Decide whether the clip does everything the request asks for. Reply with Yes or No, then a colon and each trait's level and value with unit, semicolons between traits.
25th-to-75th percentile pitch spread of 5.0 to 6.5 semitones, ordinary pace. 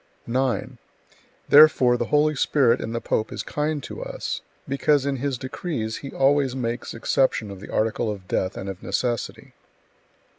No: average, 3.7 semitones; average, 160 wpm